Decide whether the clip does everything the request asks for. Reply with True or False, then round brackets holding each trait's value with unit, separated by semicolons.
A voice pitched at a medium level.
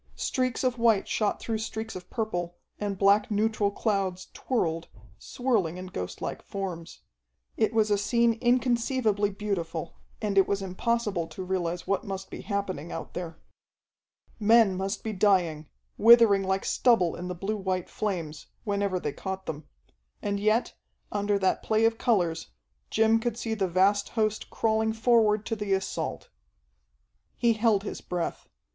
False (205 Hz)